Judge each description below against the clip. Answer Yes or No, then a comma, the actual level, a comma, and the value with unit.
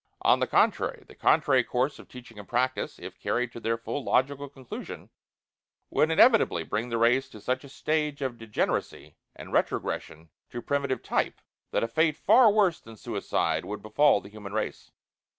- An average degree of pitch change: Yes, average, 4.0 semitones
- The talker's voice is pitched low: Yes, low, 125 Hz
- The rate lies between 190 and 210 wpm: No, average, 175 wpm